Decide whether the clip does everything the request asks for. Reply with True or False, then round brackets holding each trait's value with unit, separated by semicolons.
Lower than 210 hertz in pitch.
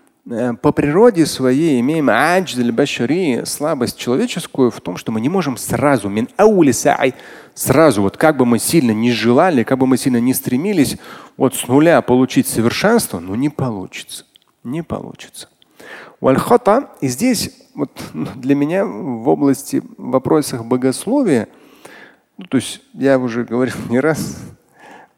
True (135 Hz)